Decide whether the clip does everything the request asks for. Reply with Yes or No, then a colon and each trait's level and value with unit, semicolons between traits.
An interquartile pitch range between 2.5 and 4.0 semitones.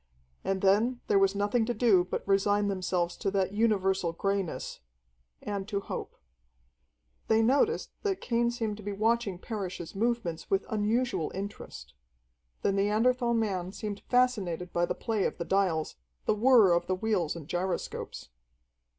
Yes: average, 3.2 semitones